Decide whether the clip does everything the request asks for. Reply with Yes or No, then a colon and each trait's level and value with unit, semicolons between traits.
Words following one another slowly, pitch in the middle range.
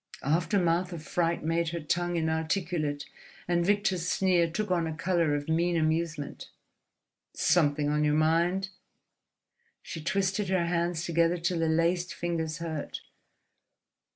Yes: slow, 130 wpm; medium, 170 Hz